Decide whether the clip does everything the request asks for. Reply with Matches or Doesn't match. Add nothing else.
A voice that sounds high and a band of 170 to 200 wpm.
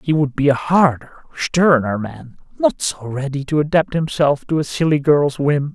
Doesn't match